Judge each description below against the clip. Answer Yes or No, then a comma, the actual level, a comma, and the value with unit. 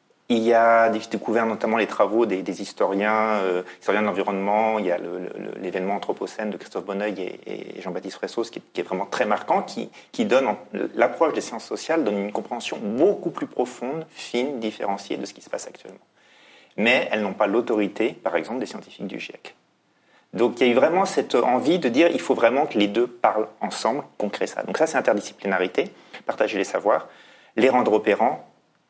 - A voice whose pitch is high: No, low, 110 Hz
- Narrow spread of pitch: Yes, narrow, 2.2 semitones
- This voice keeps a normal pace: Yes, average, 205 wpm